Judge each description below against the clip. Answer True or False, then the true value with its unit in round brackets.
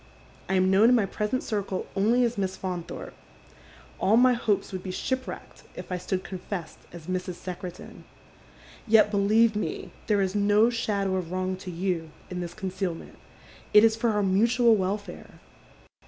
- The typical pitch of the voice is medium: False (195 Hz)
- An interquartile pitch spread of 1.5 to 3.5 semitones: True (3.0 semitones)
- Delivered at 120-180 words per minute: True (170 wpm)